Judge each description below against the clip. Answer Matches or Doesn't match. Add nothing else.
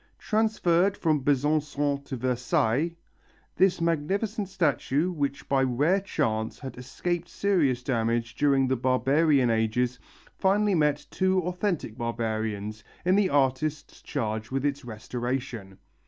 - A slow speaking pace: Matches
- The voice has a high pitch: Doesn't match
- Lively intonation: Matches